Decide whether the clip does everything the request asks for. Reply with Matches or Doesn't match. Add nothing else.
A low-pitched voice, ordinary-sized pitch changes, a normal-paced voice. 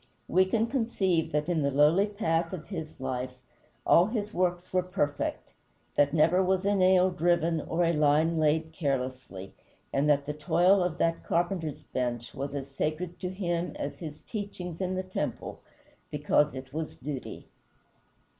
Doesn't match